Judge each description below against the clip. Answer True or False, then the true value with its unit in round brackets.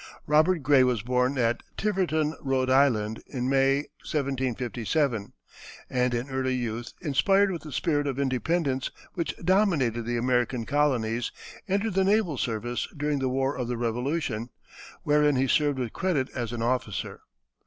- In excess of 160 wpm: False (150 wpm)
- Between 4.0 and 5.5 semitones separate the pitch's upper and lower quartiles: False (3.5 semitones)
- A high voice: False (130 Hz)